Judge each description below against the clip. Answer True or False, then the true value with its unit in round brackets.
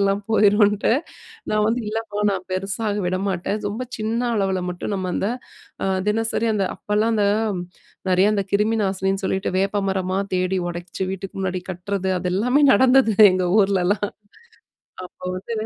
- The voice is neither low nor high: False (200 Hz)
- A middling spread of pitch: False (2.1 semitones)